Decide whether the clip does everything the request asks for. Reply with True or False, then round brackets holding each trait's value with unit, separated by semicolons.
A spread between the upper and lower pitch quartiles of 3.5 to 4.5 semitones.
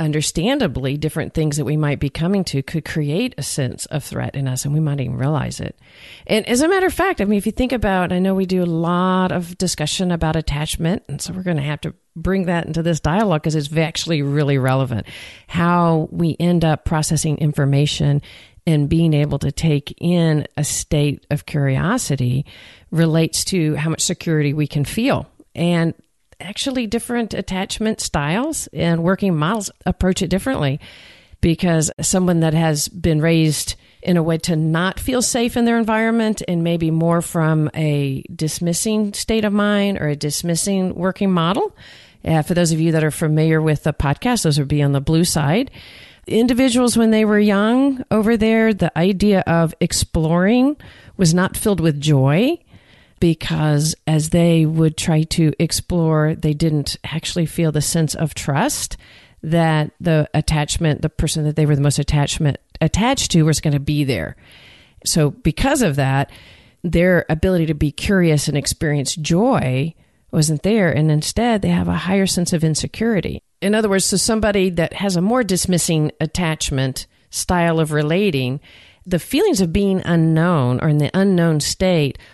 True (3.8 semitones)